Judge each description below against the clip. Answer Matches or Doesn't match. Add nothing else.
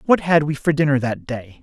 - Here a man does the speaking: Matches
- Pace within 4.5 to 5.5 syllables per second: Matches